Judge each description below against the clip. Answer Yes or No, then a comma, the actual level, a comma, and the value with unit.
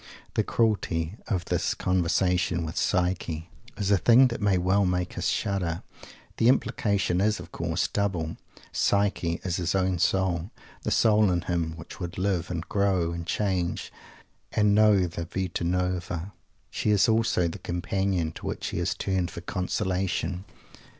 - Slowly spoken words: No, average, 155 wpm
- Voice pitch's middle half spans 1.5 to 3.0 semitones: Yes, narrow, 2.5 semitones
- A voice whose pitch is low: Yes, very low, 90 Hz